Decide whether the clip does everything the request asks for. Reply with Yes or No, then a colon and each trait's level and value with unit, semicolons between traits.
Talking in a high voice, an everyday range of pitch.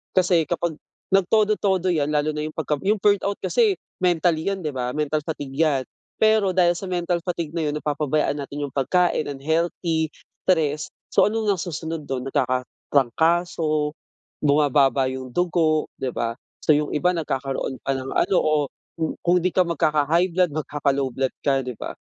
No: medium, 155 Hz; average, 3.9 semitones